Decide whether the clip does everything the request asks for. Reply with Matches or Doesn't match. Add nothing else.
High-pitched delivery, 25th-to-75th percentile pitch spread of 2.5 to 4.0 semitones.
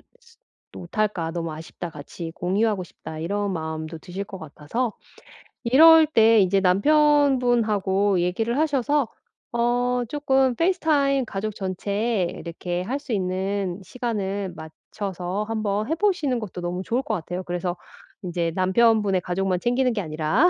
Doesn't match